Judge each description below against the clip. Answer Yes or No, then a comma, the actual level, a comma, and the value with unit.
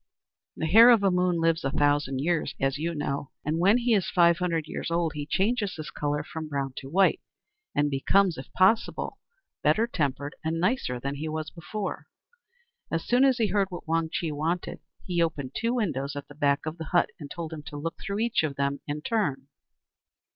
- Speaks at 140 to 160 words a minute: No, fast, 205 wpm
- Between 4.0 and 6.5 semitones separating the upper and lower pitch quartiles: Yes, average, 4.4 semitones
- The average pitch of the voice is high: No, medium, 160 Hz